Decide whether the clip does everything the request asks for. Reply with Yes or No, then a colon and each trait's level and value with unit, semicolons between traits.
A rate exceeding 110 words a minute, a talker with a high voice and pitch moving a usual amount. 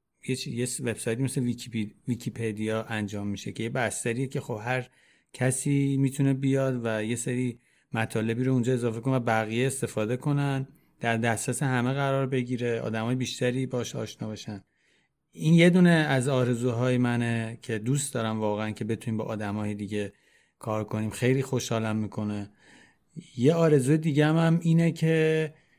No: average, 150 wpm; low, 125 Hz; average, 3.4 semitones